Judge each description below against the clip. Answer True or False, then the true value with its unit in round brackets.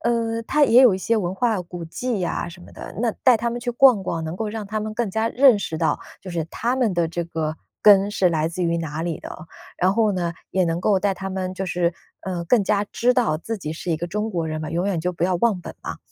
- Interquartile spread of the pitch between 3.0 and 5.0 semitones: True (4.7 semitones)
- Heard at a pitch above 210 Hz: False (190 Hz)